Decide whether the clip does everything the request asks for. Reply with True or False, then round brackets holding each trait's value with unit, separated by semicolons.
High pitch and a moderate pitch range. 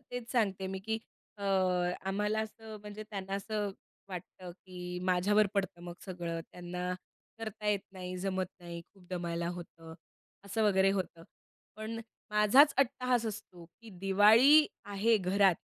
True (195 Hz; 3.2 semitones)